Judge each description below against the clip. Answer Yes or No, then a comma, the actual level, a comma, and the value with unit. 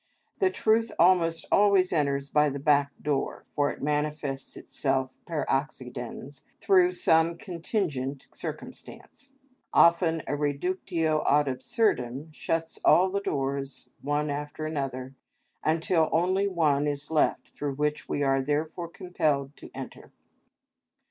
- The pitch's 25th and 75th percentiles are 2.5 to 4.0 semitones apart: Yes, average, 3.3 semitones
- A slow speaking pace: Yes, slow, 125 wpm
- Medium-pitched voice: Yes, medium, 150 Hz